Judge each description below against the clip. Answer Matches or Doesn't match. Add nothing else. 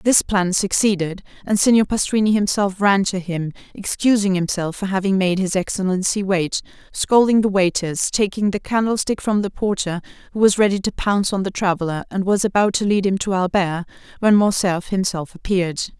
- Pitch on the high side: Matches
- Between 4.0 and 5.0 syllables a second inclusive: Doesn't match